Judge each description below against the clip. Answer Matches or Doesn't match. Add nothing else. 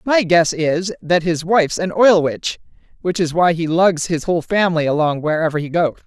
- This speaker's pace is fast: Matches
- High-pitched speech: Doesn't match